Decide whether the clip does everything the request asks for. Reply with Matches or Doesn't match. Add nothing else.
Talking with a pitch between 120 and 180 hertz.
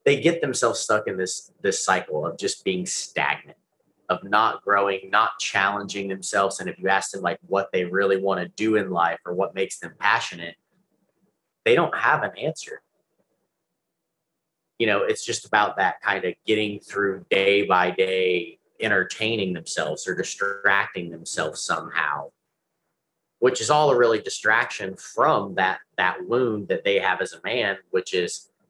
Doesn't match